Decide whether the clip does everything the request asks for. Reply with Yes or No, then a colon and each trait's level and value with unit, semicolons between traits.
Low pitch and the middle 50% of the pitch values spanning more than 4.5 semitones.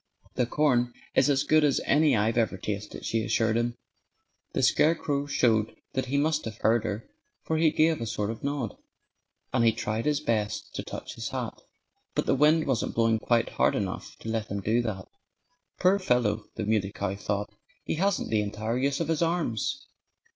Yes: low, 120 Hz; average, 5.3 semitones